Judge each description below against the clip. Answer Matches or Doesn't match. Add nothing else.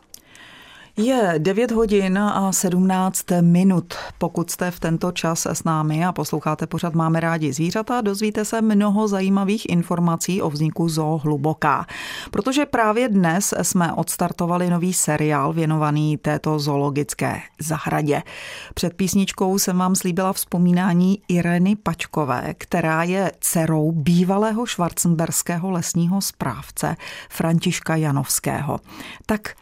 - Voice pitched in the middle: Matches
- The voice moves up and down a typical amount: Matches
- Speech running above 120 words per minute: Doesn't match